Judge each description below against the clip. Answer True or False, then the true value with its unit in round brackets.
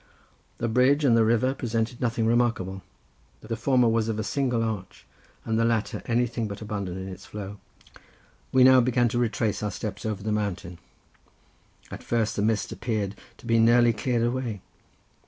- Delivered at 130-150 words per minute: False (175 wpm)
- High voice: False (115 Hz)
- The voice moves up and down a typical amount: False (2.3 semitones)